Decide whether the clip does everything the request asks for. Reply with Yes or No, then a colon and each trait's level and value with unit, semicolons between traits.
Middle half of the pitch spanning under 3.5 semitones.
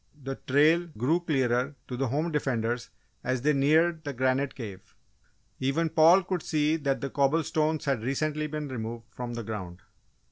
No: average, 3.8 semitones